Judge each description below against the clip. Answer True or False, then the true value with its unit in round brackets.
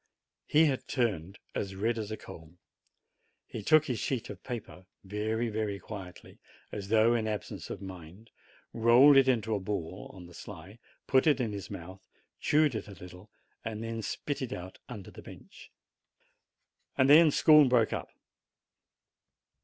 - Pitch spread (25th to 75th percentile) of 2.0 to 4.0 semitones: False (4.5 semitones)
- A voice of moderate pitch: False (110 Hz)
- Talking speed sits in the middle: True (160 wpm)